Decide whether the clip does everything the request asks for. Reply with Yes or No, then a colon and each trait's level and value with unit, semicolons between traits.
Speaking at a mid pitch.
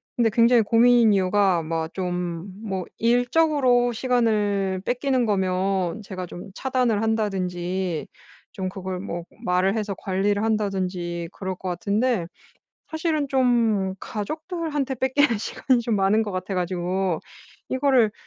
No: high, 205 Hz